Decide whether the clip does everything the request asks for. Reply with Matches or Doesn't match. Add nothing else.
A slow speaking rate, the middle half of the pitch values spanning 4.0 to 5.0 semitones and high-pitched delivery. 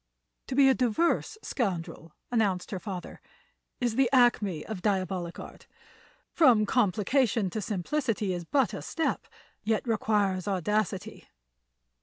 Matches